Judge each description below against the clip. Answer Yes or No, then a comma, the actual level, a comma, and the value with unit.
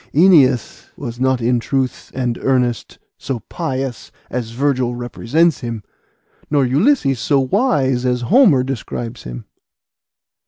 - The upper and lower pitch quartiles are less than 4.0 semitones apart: Yes, average, 2.7 semitones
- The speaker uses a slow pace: Yes, slow, 120 wpm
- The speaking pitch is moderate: No, low, 130 Hz